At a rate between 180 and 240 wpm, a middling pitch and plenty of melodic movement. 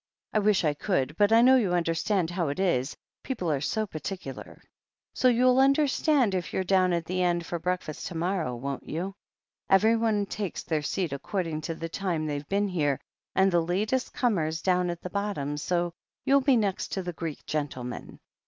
No: average, 195 wpm; medium, 180 Hz; average, 4.4 semitones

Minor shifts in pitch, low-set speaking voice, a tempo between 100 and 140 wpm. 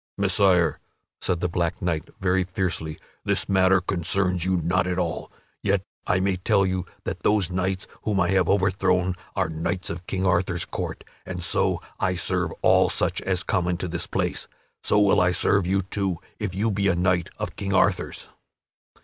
No: narrow, 1.6 semitones; very low, 90 Hz; average, 180 wpm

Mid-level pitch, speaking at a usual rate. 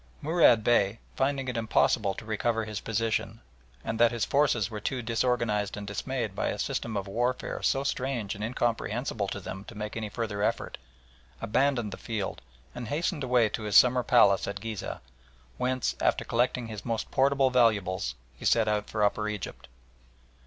No: low, 115 Hz; average, 175 wpm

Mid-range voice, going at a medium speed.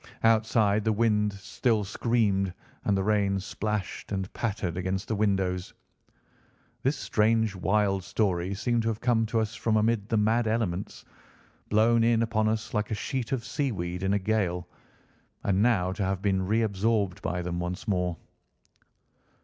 No: low, 105 Hz; average, 155 wpm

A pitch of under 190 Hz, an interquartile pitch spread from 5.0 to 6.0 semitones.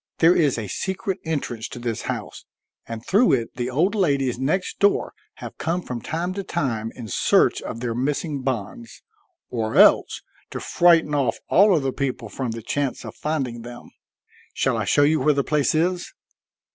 Yes: medium, 140 Hz; wide, 5.5 semitones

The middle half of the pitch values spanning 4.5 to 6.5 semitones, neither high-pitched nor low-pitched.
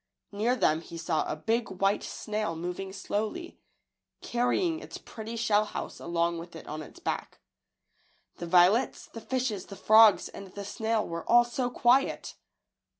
No: average, 5.1 semitones; high, 210 Hz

